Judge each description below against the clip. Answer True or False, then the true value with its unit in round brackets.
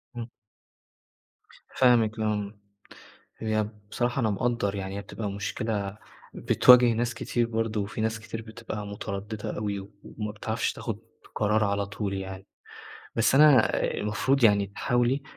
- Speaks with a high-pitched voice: False (110 Hz)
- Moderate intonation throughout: False (2.3 semitones)